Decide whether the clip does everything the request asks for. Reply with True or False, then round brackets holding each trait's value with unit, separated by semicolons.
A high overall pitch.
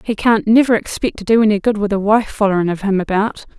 True (205 Hz)